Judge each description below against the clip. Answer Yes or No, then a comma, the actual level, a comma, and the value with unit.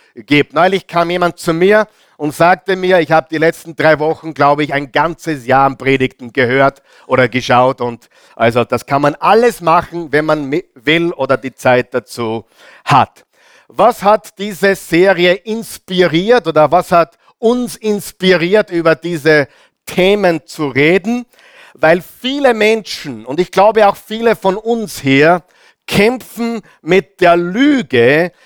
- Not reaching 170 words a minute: Yes, average, 150 wpm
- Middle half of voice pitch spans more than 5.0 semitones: Yes, wide, 5.4 semitones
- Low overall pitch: No, medium, 170 Hz